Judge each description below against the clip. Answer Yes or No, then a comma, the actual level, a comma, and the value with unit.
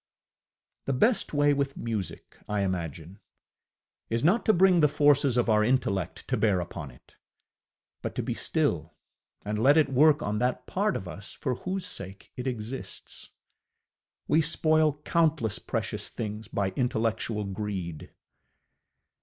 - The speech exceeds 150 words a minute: No, average, 145 wpm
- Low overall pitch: Yes, low, 120 Hz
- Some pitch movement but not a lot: No, wide, 6.3 semitones